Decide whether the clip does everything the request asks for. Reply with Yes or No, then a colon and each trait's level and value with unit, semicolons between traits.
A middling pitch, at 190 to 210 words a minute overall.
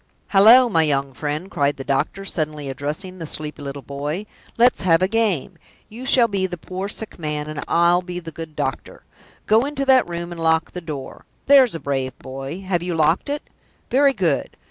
Yes: medium, 170 Hz; average, 195 wpm